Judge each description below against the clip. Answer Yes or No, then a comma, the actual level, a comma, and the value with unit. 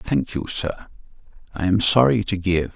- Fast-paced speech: No, average, 175 wpm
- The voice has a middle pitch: No, very low, 90 Hz